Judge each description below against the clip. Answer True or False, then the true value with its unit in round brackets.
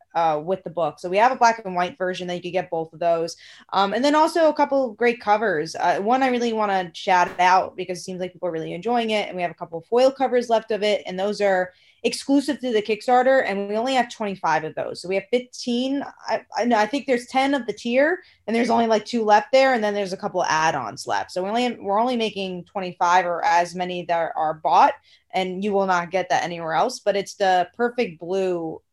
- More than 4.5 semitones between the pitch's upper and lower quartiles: True (5.1 semitones)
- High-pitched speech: True (200 Hz)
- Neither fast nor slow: False (255 wpm)